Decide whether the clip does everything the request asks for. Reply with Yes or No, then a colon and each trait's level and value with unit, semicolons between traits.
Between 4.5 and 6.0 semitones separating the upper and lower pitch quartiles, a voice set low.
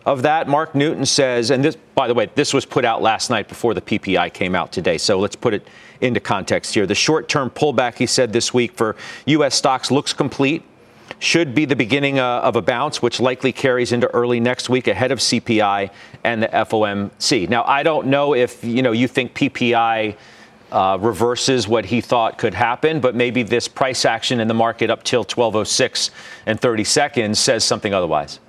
No: average, 2.8 semitones; low, 125 Hz